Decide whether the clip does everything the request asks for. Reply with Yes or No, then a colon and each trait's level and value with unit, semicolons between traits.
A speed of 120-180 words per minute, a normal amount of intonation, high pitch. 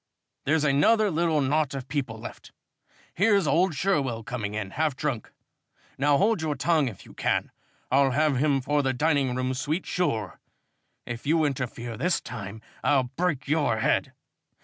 No: average, 160 wpm; average, 3.9 semitones; medium, 140 Hz